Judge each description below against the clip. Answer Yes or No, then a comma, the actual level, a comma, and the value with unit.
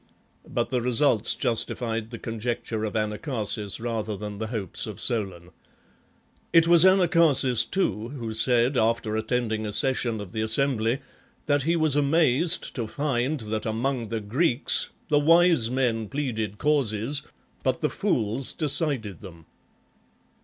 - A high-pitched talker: No, low, 120 Hz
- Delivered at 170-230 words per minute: No, average, 140 wpm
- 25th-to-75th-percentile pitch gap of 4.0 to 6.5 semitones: Yes, average, 4.6 semitones